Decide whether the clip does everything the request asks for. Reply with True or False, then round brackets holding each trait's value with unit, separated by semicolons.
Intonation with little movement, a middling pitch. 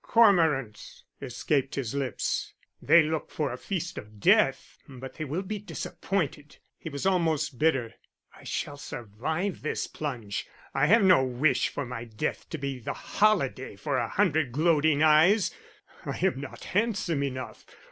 False (4.7 semitones; 150 Hz)